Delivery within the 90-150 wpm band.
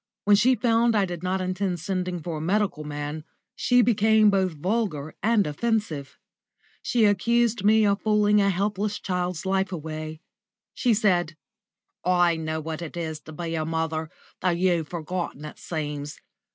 No: average, 160 wpm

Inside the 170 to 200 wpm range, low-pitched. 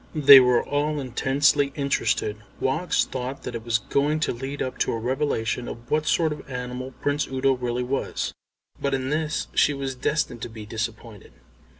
Yes: average, 180 wpm; low, 130 Hz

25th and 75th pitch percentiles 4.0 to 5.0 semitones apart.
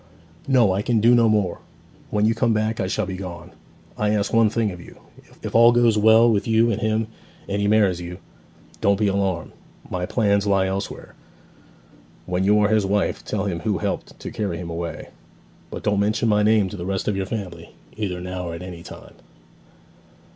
No: average, 2.8 semitones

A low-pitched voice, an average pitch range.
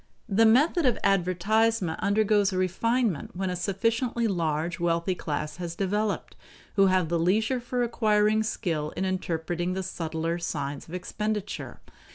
No: high, 190 Hz; average, 4.2 semitones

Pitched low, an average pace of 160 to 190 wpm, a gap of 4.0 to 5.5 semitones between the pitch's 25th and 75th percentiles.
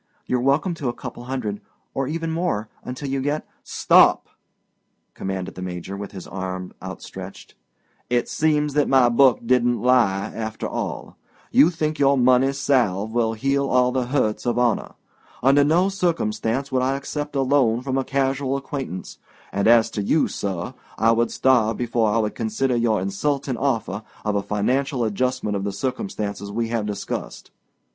Yes: low, 125 Hz; average, 165 wpm; average, 4.3 semitones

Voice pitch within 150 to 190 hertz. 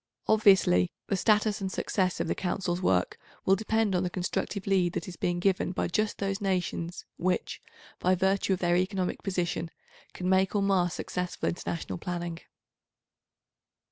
Yes: medium, 185 Hz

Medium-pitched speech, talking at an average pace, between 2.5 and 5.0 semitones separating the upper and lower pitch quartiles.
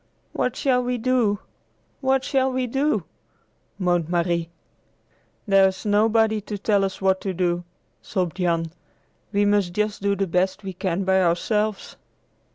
No: high, 200 Hz; average, 145 wpm; average, 3.3 semitones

